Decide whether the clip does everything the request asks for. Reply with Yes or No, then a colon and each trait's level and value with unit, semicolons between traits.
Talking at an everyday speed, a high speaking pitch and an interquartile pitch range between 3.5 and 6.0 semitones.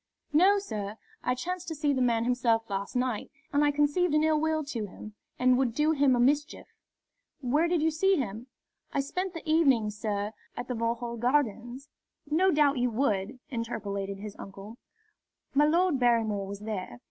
Yes: average, 180 wpm; very high, 250 Hz; wide, 5.4 semitones